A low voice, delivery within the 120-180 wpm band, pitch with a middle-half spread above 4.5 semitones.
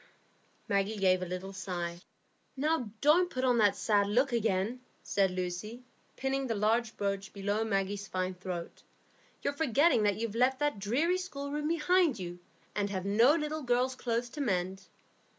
No: high, 220 Hz; average, 160 wpm; wide, 5.5 semitones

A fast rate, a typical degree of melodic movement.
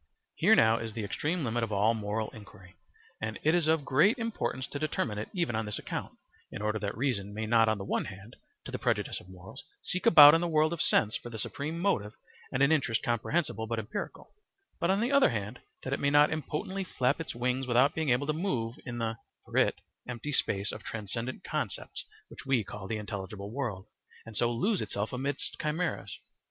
No: fast, 215 wpm; wide, 5.8 semitones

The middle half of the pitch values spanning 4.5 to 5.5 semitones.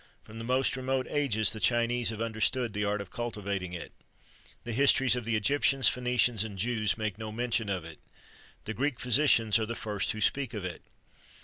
No: average, 2.9 semitones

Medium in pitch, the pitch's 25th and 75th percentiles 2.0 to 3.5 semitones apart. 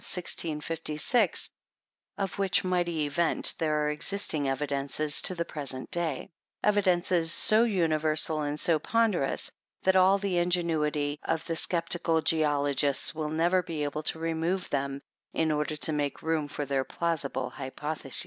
Yes: medium, 160 Hz; average, 2.8 semitones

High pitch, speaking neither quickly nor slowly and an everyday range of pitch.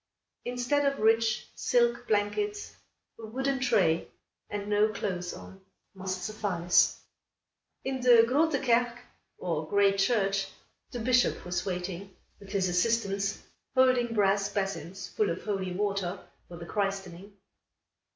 No: high, 205 Hz; slow, 125 wpm; average, 3.9 semitones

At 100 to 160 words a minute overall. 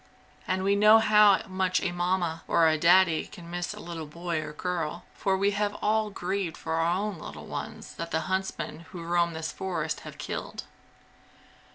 No: average, 185 wpm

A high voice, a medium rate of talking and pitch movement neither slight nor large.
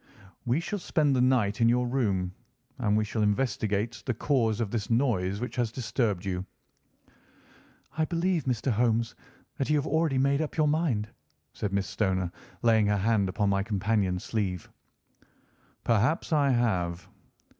No: low, 115 Hz; average, 155 wpm; average, 4.7 semitones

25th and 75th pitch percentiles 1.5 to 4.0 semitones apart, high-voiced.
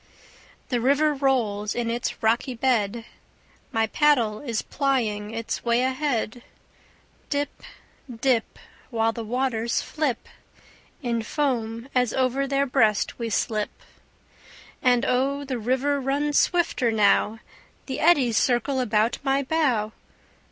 Yes: average, 3.4 semitones; high, 245 Hz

